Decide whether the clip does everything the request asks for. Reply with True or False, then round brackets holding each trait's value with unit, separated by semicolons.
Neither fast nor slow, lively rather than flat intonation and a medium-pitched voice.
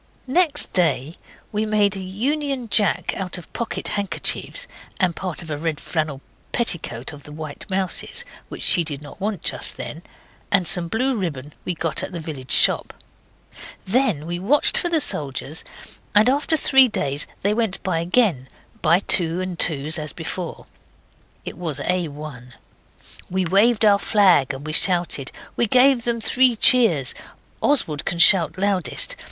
True (160 wpm; 5.9 semitones; 180 Hz)